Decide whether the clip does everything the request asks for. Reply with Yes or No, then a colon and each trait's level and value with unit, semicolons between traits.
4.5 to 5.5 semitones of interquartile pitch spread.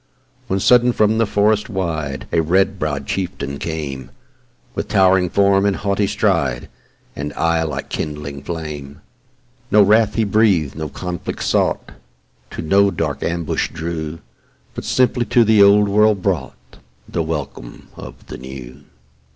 Yes: average, 5.2 semitones